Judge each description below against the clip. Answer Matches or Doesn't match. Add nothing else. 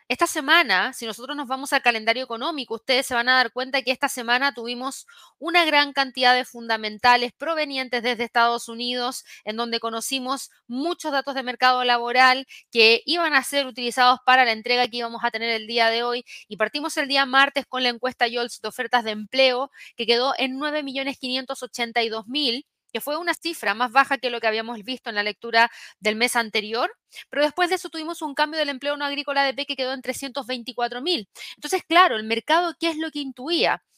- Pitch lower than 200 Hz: Doesn't match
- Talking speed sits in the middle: Doesn't match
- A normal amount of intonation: Matches